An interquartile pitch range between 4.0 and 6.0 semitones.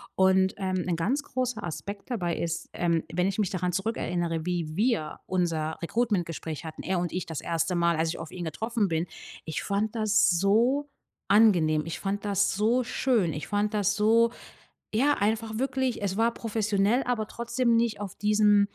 Yes: average, 4.5 semitones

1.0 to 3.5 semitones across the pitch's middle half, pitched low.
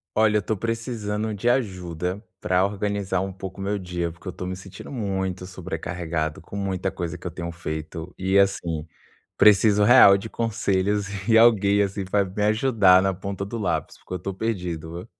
Yes: narrow, 2.5 semitones; very low, 95 Hz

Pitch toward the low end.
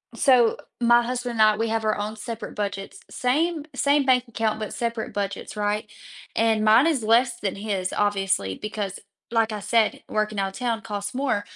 No: high, 220 Hz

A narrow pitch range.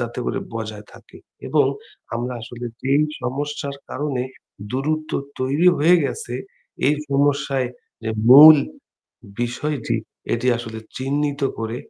No: average, 3.3 semitones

